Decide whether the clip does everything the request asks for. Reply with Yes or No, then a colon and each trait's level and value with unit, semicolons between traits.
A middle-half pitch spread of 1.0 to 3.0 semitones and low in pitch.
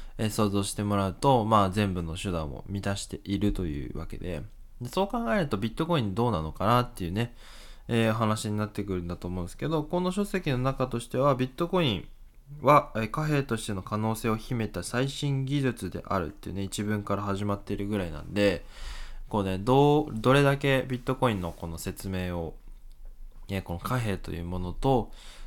No: average, 4.9 semitones; low, 110 Hz